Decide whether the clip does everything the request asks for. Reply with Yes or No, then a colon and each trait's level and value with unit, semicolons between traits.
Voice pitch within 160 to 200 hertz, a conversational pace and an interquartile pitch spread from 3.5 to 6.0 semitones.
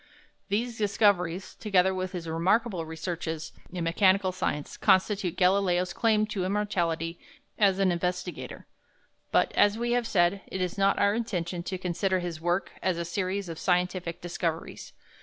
No: medium, 185 Hz; average, 150 wpm; narrow, 2.6 semitones